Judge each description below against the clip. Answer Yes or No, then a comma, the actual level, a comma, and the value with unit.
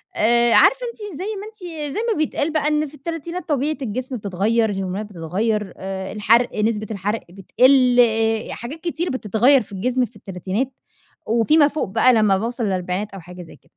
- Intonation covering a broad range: Yes, wide, 6.3 semitones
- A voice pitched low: No, high, 235 Hz